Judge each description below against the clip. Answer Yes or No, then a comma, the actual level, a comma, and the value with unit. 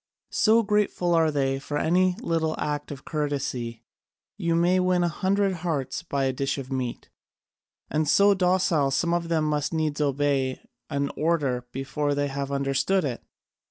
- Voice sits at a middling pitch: Yes, medium, 150 Hz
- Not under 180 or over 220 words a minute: No, average, 160 wpm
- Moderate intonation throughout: Yes, average, 4.0 semitones